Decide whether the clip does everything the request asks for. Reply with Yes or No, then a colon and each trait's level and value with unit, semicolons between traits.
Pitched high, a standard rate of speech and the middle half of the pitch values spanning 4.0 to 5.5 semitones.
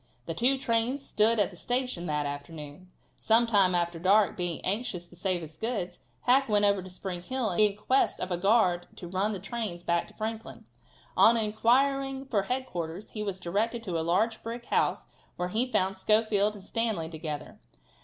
Yes: high, 205 Hz; average, 185 wpm; average, 4.6 semitones